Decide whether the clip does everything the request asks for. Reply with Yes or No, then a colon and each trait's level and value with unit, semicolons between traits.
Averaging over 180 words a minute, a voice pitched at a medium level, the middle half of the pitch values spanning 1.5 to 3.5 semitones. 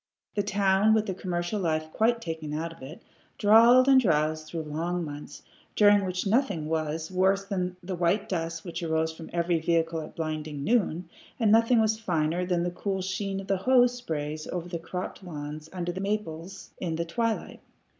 No: average, 190 wpm; medium, 175 Hz; average, 3.9 semitones